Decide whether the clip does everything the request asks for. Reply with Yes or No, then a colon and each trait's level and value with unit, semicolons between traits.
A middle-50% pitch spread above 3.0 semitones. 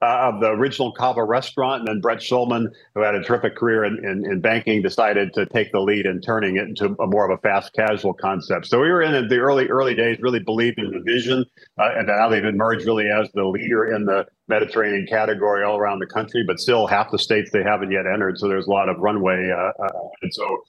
No: narrow, 2.6 semitones